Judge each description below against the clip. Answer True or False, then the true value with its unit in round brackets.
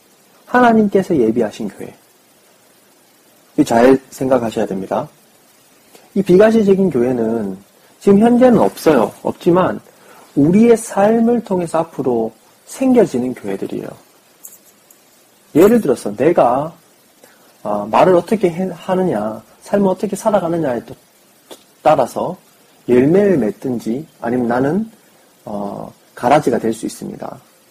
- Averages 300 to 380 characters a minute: False (240 characters per minute)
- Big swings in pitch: True (8.8 semitones)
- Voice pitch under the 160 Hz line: False (175 Hz)